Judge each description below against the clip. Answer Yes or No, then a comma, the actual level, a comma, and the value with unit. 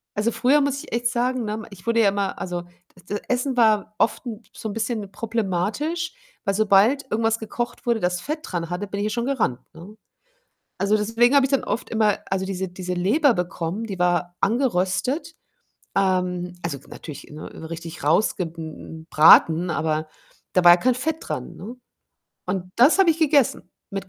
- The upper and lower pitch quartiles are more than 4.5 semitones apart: Yes, average, 5.2 semitones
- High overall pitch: Yes, high, 205 Hz